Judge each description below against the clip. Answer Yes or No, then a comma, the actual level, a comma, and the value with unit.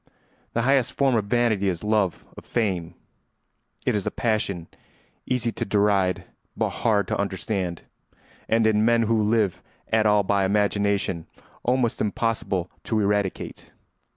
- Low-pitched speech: Yes, low, 105 Hz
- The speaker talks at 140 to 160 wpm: Yes, average, 145 wpm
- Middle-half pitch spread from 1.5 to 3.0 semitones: Yes, average, 2.7 semitones